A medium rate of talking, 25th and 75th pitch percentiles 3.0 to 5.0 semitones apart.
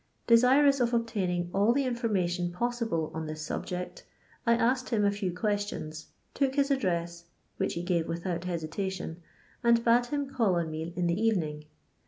No: average, 165 wpm; wide, 5.6 semitones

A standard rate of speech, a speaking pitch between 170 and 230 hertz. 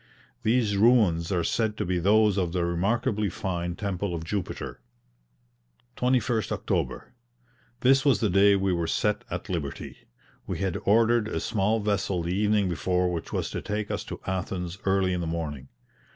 No: average, 165 wpm; very low, 95 Hz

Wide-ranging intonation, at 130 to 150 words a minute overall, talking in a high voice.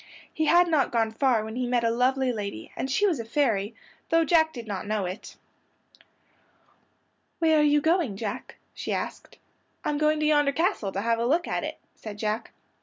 No: wide, 5.7 semitones; average, 195 wpm; very high, 250 Hz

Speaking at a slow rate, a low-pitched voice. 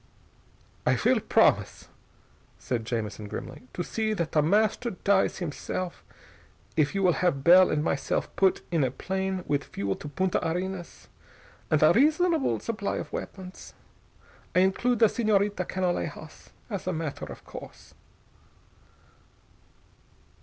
No: slow, 130 wpm; medium, 185 Hz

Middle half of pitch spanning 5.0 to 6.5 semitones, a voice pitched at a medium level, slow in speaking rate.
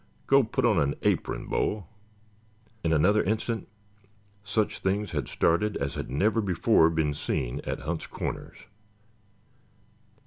No: wide, 5.4 semitones; very low, 95 Hz; slow, 130 wpm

